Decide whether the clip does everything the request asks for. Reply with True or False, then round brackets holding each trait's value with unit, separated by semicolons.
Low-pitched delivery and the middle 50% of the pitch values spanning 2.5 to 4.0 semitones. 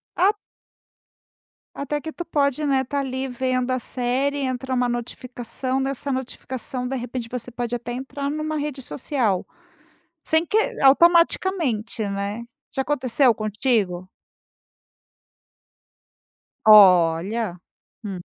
False (255 Hz; 3.4 semitones)